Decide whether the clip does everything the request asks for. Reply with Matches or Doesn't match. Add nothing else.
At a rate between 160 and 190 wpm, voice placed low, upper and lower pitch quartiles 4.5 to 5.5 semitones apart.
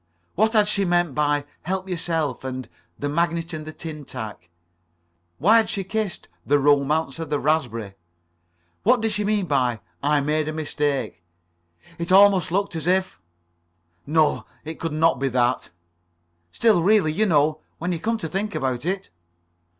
Doesn't match